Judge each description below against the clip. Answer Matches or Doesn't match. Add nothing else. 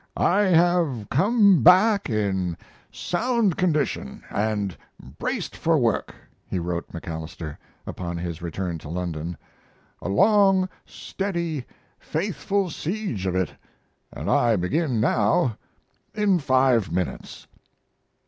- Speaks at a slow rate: Matches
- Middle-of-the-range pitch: Doesn't match